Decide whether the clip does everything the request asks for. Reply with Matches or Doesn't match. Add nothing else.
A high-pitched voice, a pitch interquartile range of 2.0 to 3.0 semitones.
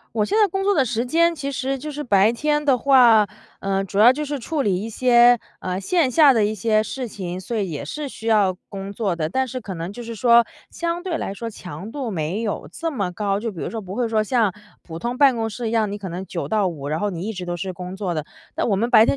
Doesn't match